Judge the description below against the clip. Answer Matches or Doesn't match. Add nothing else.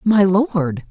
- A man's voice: Doesn't match